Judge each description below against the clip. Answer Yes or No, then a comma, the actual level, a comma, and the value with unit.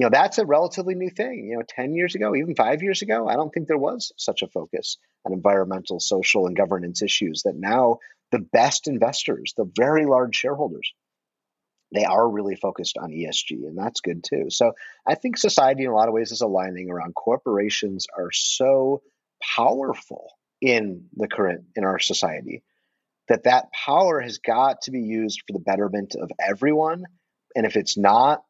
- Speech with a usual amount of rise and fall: No, wide, 7.6 semitones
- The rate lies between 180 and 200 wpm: Yes, average, 185 wpm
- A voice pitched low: Yes, low, 115 Hz